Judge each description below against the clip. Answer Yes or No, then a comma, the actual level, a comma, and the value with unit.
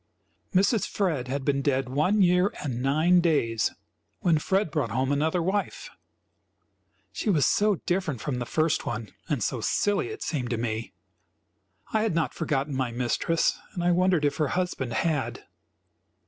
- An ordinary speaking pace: Yes, average, 160 wpm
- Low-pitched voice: No, medium, 150 Hz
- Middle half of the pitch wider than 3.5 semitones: Yes, wide, 5.6 semitones